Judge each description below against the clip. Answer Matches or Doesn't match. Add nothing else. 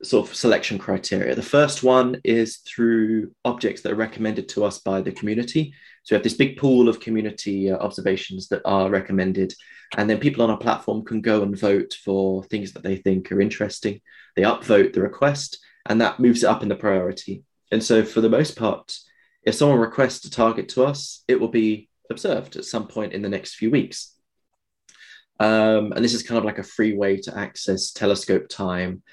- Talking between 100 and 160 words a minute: Doesn't match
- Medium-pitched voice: Doesn't match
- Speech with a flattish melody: Doesn't match